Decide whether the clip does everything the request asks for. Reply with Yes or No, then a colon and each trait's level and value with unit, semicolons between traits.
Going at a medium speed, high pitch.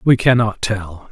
No: average, 160 wpm; low, 110 Hz